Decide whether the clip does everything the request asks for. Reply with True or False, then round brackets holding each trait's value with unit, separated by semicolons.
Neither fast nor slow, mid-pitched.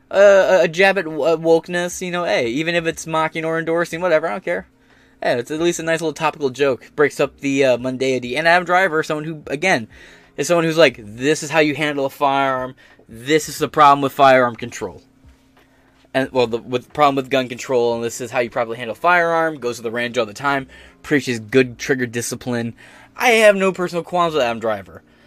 False (225 wpm; 145 Hz)